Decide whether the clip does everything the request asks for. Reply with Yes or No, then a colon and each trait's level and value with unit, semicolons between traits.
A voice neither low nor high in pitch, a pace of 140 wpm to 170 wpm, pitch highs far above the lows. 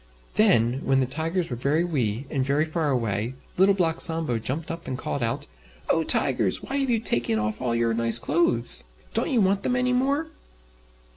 No: medium, 150 Hz; average, 195 wpm; wide, 8.1 semitones